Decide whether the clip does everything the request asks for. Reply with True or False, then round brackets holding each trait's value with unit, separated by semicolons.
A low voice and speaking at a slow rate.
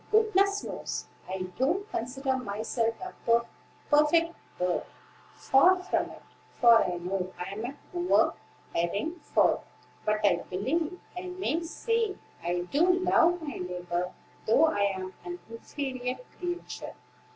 False (260 Hz; 130 wpm)